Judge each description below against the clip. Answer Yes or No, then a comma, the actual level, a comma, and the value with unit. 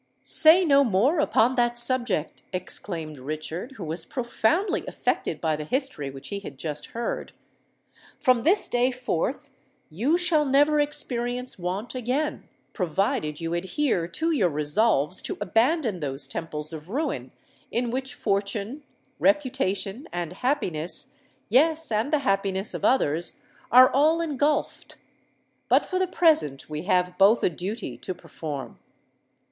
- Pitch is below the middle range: No, high, 225 Hz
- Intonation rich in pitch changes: Yes, wide, 8.1 semitones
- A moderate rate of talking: No, slow, 130 wpm